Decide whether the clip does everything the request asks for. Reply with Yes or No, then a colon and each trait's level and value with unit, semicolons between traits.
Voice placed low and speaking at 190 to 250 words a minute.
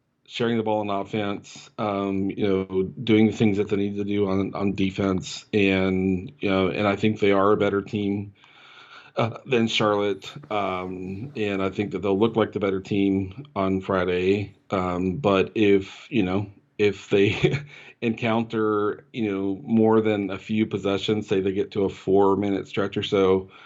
No: low, 100 Hz; average, 180 wpm